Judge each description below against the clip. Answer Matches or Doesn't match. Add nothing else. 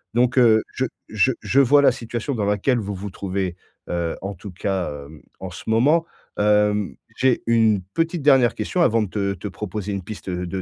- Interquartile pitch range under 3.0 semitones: Doesn't match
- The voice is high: Doesn't match